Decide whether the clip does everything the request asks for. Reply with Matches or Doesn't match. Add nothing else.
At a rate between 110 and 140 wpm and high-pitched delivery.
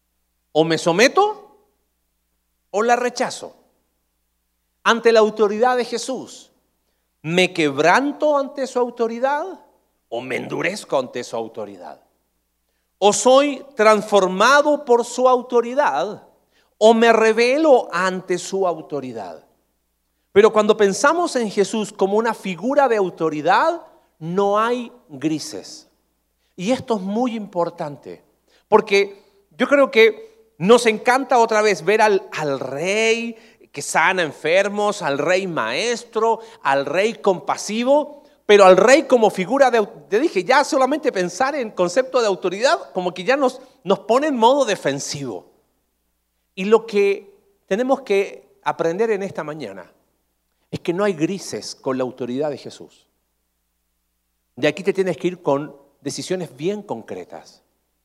Matches